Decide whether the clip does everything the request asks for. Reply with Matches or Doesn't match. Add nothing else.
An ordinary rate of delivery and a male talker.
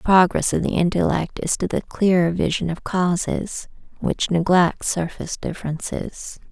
Doesn't match